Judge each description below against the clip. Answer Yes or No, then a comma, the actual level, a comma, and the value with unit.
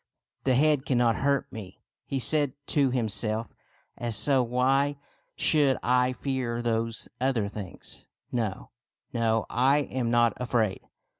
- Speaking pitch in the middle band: No, low, 125 Hz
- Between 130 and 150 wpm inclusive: Yes, average, 140 wpm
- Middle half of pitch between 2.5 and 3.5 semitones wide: Yes, average, 2.9 semitones